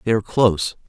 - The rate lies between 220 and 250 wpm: No, fast, 205 wpm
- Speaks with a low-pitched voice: Yes, low, 105 Hz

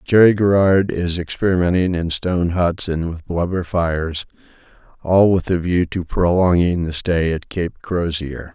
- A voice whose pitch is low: Yes, very low, 85 Hz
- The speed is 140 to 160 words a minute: Yes, average, 145 wpm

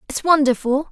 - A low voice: No, very high, 280 Hz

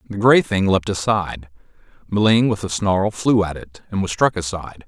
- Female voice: No, male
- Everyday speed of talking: Yes, average, 195 wpm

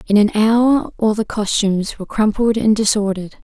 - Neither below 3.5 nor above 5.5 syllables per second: Yes, 5.4 syllables/s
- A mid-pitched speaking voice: No, high, 210 Hz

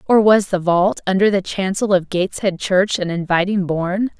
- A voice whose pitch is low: No, high, 190 Hz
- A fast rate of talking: No, average, 185 wpm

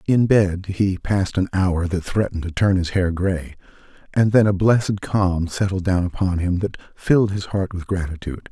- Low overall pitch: Yes, very low, 95 Hz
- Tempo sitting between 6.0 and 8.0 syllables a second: No, 5.0 syllables/s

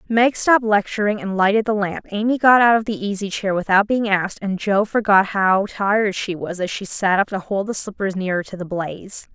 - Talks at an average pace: No, fast, 230 wpm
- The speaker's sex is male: No, female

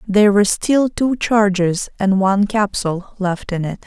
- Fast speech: No, average, 170 wpm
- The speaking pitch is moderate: No, high, 200 Hz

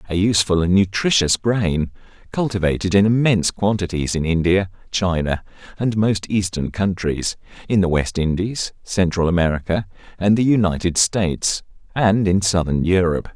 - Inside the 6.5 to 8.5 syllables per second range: No, 5.0 syllables/s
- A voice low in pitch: Yes, very low, 95 Hz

